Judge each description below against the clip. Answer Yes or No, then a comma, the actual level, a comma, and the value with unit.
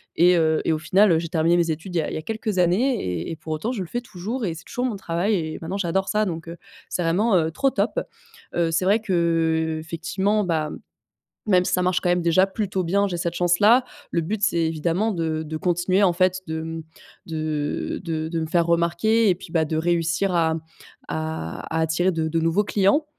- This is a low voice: No, medium, 170 Hz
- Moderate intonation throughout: Yes, average, 3.1 semitones